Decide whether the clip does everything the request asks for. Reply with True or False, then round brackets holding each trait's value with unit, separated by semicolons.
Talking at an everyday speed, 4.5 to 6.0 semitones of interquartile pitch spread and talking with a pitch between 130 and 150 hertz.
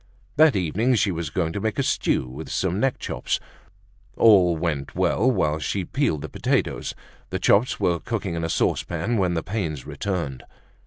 False (175 wpm; 5.1 semitones; 90 Hz)